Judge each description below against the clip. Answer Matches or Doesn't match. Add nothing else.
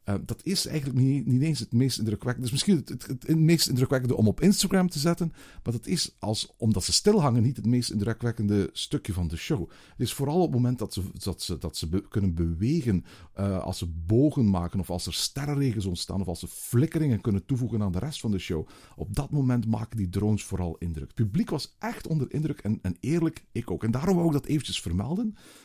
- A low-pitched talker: Matches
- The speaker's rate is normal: Doesn't match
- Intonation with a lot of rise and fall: Matches